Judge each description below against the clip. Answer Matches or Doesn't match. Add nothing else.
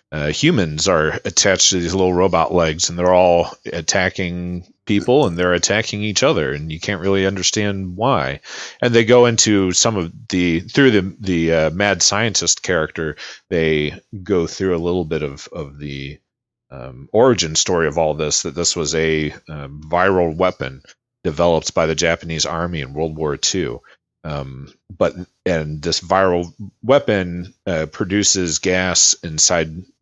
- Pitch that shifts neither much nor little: Matches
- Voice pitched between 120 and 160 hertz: Doesn't match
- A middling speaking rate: Matches